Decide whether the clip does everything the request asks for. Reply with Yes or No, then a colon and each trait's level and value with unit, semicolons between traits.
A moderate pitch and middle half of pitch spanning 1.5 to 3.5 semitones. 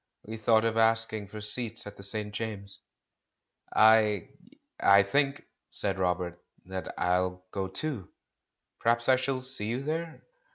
No: low, 110 Hz; average, 3.1 semitones